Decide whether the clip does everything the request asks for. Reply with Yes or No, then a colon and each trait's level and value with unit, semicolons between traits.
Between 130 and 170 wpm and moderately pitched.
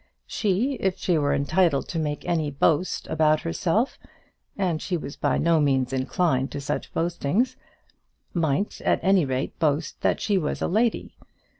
Yes: average, 160 wpm; medium, 165 Hz